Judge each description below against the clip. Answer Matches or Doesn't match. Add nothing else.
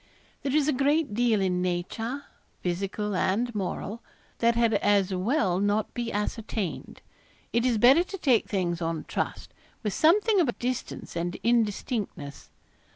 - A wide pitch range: Doesn't match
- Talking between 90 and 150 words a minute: Matches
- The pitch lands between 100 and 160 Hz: Doesn't match